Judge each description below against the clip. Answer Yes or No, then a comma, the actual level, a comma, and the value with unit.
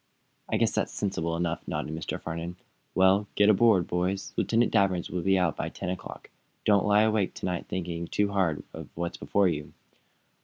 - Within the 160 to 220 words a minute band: Yes, average, 185 wpm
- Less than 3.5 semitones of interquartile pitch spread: Yes, average, 2.9 semitones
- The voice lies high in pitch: No, very low, 95 Hz